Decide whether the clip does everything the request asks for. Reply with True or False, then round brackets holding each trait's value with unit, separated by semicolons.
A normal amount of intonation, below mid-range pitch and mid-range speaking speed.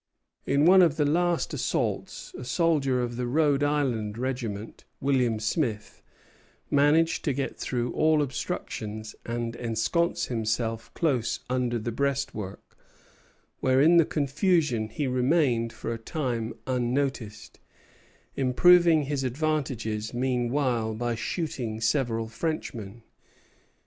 False (4.4 semitones; 125 Hz; 115 wpm)